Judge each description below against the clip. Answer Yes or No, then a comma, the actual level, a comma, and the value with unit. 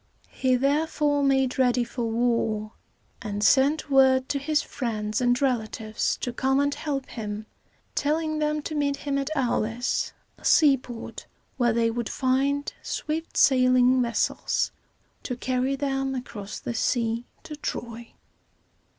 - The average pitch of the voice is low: No, very high, 260 Hz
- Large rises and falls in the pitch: No, average, 3.1 semitones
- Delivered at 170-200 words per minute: No, slow, 135 wpm